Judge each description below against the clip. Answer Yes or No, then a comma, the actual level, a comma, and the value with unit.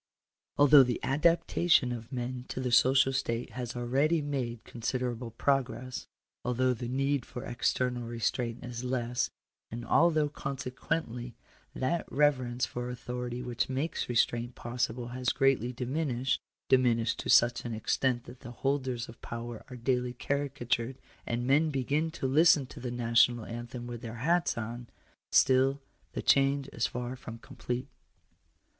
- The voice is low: Yes, low, 125 Hz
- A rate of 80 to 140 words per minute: No, average, 160 wpm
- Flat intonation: Yes, narrow, 2.1 semitones